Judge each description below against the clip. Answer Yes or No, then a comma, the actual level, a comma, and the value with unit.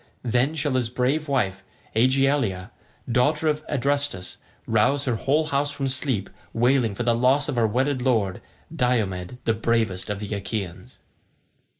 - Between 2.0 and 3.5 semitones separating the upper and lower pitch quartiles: No, average, 4.2 semitones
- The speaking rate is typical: Yes, average, 145 wpm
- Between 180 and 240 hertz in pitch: No, low, 125 Hz